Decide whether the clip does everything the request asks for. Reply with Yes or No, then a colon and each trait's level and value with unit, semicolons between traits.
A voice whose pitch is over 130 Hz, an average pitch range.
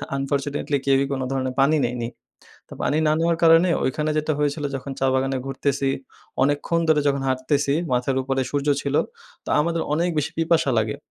No: medium, 140 Hz; narrow, 2.3 semitones